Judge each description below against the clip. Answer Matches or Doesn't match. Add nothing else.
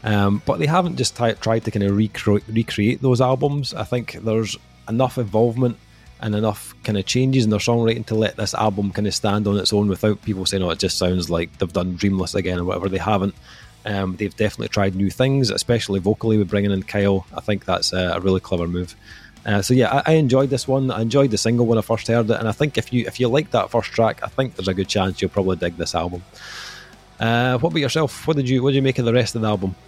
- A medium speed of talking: Doesn't match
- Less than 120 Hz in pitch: Matches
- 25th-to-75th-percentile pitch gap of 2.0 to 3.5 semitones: Doesn't match